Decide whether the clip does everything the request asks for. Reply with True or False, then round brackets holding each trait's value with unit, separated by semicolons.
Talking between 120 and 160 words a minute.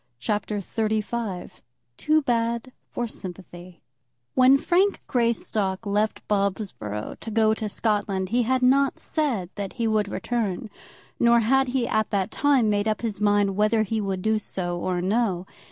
True (155 wpm)